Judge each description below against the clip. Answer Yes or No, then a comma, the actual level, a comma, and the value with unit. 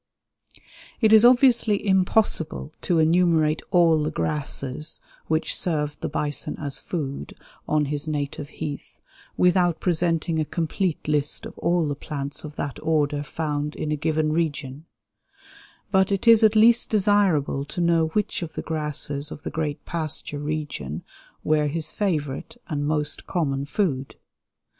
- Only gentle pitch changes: No, average, 3.2 semitones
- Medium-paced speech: Yes, average, 145 wpm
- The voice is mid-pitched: Yes, medium, 155 Hz